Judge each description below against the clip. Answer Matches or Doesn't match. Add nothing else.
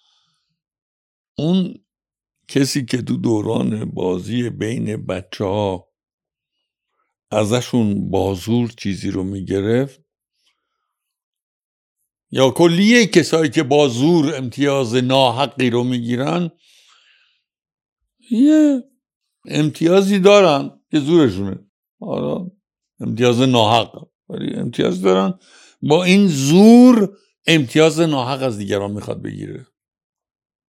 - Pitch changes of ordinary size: Doesn't match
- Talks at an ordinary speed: Doesn't match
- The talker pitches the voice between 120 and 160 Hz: Matches